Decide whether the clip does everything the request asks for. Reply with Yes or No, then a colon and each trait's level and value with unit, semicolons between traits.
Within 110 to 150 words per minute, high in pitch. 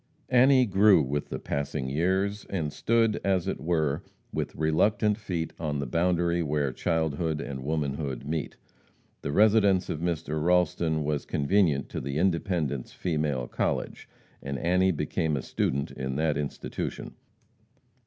No: average, 140 wpm; very low, 80 Hz